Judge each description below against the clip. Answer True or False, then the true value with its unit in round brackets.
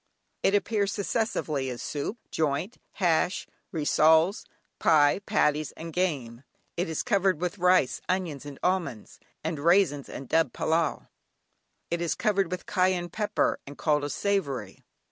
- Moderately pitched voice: True (165 Hz)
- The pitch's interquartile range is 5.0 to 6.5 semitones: False (4.3 semitones)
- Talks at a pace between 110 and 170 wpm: True (140 wpm)